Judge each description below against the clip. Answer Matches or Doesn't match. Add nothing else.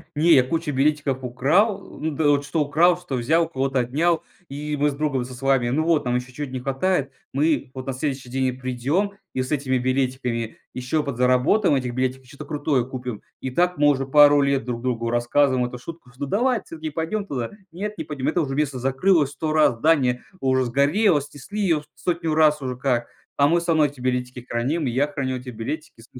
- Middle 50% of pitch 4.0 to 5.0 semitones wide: Doesn't match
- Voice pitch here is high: Doesn't match